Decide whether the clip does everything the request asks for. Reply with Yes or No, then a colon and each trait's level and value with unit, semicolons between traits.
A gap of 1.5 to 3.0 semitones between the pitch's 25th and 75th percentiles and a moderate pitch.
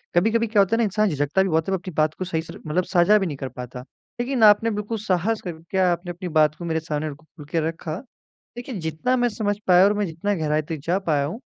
No: average, 4.7 semitones; medium, 180 Hz